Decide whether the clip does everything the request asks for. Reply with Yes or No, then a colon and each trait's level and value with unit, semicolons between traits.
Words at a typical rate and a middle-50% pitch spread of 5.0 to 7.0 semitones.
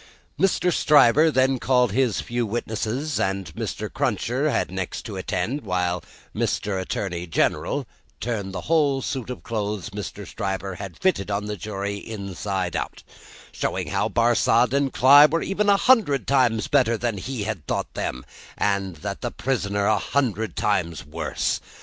Yes: average, 155 wpm; average, 5.3 semitones